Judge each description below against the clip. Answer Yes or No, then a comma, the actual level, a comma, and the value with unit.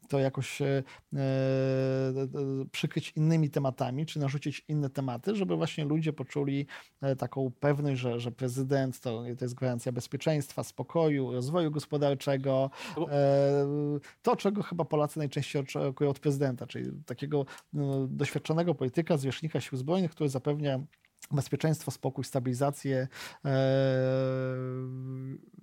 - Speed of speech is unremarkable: Yes, average, 120 wpm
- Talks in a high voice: No, medium, 140 Hz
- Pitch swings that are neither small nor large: No, narrow, 2.3 semitones